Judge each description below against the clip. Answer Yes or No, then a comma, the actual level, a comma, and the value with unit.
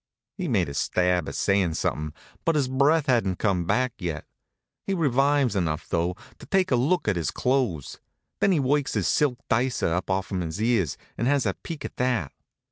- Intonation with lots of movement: Yes, wide, 7.6 semitones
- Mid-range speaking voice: No, low, 120 Hz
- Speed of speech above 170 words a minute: Yes, average, 195 wpm